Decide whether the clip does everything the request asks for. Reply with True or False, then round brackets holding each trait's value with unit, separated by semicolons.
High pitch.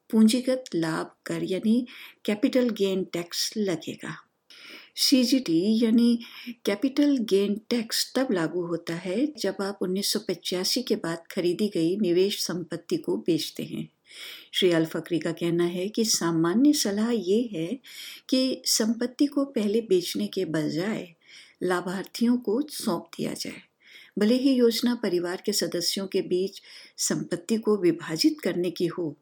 True (205 Hz)